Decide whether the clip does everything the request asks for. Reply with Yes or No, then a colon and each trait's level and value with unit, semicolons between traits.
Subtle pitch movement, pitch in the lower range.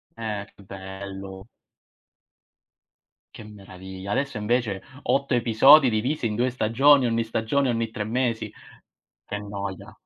No: average, 3.6 semitones; low, 110 Hz